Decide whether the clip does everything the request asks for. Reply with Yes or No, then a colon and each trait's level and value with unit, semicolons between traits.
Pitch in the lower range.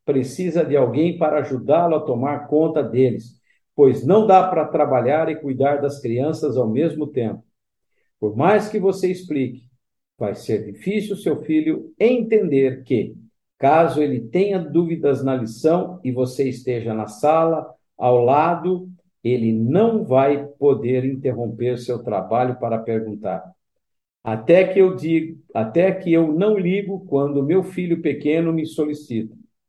No: medium, 150 Hz